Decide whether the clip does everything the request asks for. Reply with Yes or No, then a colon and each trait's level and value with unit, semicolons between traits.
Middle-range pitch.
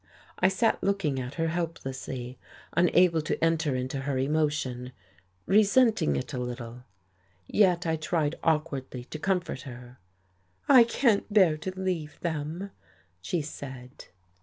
Yes: medium, 155 Hz